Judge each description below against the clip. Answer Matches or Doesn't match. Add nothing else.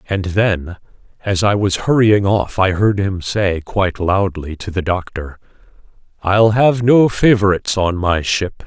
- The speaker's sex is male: Matches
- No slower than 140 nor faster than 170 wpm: Matches